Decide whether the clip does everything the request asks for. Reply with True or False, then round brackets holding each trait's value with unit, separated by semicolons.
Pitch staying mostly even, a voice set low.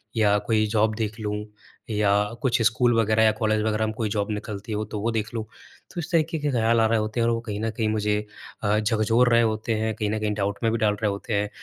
True (1.4 semitones; 110 Hz)